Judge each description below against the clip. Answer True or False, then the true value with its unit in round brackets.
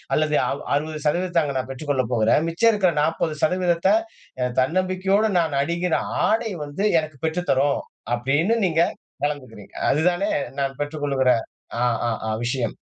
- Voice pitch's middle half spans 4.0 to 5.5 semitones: True (4.5 semitones)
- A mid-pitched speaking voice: True (155 Hz)